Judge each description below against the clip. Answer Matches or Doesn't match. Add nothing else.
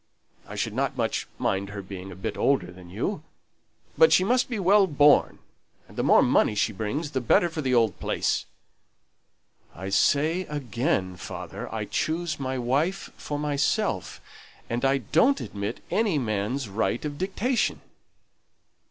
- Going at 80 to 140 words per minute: Doesn't match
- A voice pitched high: Doesn't match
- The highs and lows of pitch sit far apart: Matches